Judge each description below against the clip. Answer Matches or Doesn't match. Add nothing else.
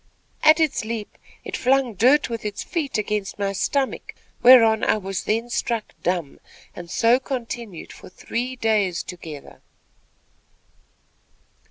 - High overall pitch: Matches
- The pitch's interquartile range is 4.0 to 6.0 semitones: Matches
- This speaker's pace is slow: Matches